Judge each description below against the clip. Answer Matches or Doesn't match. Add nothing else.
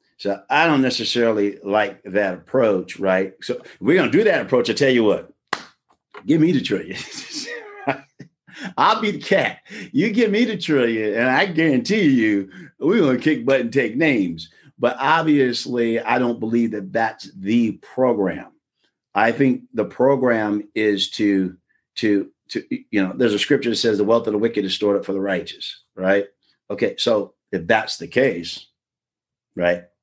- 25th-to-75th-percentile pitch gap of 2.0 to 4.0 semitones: Doesn't match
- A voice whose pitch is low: Matches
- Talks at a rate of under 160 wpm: Doesn't match